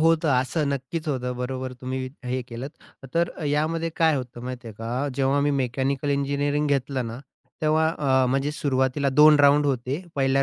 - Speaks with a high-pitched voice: No, low, 135 Hz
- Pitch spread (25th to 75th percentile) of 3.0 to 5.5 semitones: No, narrow, 2.4 semitones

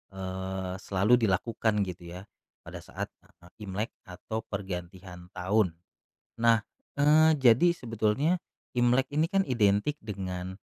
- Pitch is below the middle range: Yes, low, 105 Hz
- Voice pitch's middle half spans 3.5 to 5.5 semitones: Yes, average, 4.6 semitones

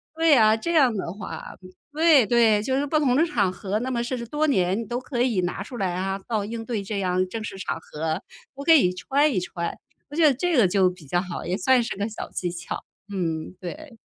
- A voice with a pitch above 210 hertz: Yes, high, 220 Hz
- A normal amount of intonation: No, wide, 6.0 semitones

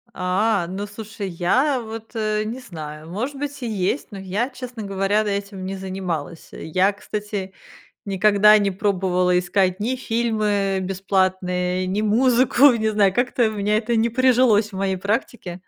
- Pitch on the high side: Yes, high, 205 Hz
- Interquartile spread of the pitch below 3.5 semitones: Yes, average, 3.1 semitones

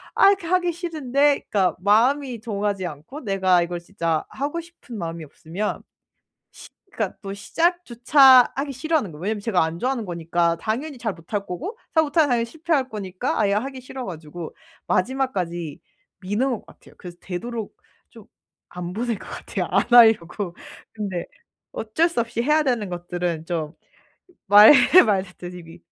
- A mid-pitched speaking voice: No, high, 210 Hz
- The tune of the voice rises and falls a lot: Yes, wide, 6.9 semitones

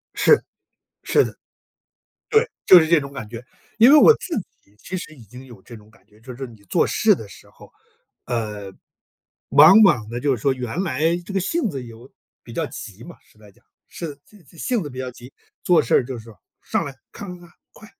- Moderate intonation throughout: No, wide, 7.4 semitones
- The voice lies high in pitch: No, low, 135 Hz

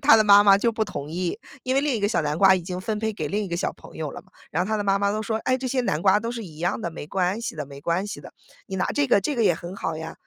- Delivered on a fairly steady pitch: No, average, 4.2 semitones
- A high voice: Yes, high, 200 Hz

